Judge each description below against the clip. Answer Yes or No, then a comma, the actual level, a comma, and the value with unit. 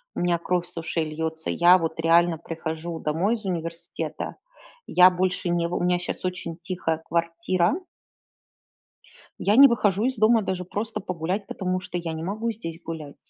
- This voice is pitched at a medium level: Yes, medium, 175 Hz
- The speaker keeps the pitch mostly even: Yes, narrow, 2.2 semitones